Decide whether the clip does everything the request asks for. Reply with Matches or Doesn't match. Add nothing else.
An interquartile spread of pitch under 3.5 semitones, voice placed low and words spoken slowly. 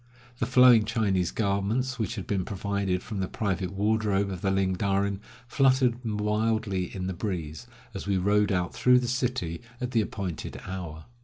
Doesn't match